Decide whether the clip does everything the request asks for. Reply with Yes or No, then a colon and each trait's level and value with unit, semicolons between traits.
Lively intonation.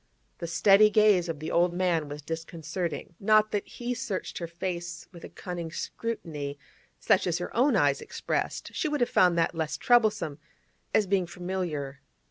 No: average, 4.0 semitones